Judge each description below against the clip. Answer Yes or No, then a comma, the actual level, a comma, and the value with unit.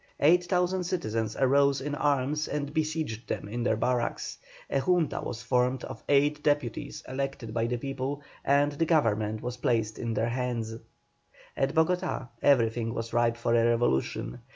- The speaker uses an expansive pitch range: No, average, 4.0 semitones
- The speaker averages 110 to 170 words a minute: Yes, average, 160 wpm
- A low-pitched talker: Yes, low, 130 Hz